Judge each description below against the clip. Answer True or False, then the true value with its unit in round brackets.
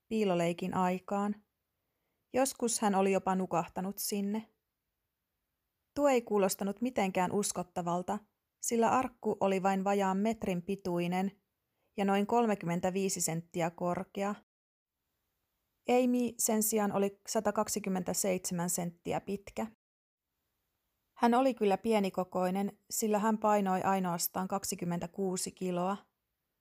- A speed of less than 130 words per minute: True (95 wpm)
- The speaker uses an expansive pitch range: False (2.7 semitones)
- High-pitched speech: True (195 Hz)